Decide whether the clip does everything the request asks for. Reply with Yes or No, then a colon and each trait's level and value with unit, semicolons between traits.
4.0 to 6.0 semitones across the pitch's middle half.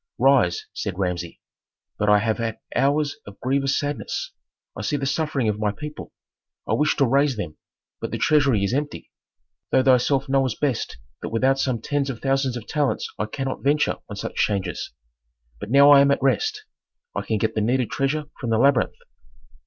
Yes: average, 4.5 semitones